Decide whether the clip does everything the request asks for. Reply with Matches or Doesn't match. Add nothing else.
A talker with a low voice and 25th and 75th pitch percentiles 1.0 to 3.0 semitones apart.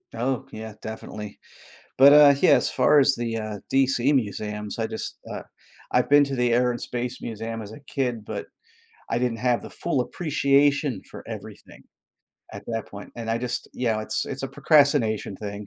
Doesn't match